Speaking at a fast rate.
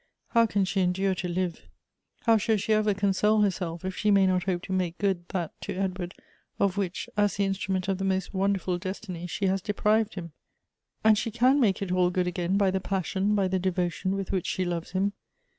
Yes: fast, 220 wpm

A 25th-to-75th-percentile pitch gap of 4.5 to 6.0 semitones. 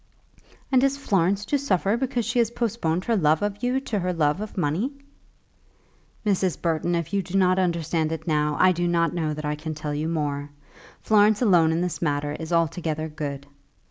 Yes: average, 4.8 semitones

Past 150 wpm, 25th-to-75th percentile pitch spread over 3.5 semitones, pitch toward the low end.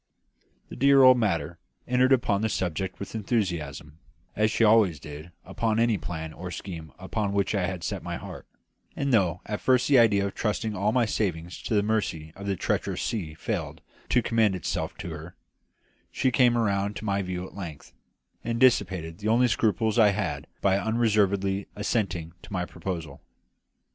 Yes: average, 180 wpm; average, 4.1 semitones; low, 100 Hz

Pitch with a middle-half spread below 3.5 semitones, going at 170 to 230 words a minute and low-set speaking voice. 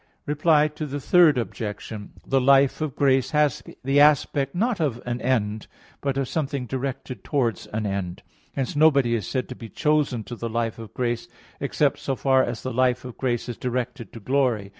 Yes: average, 3.1 semitones; average, 180 wpm; low, 130 Hz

